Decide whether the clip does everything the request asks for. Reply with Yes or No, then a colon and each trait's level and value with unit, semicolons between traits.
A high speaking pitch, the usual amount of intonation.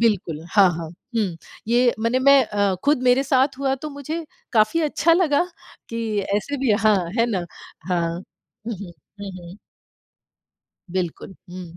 No: high, 230 Hz; wide, 6.3 semitones